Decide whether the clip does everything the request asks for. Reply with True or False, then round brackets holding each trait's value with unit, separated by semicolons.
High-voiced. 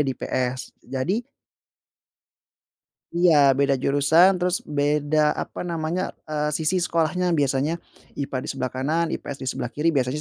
False (150 Hz)